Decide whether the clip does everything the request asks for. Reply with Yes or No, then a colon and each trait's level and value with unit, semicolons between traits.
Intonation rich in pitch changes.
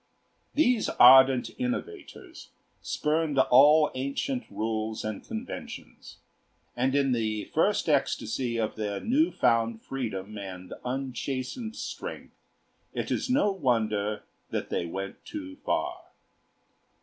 Yes: wide, 6.5 semitones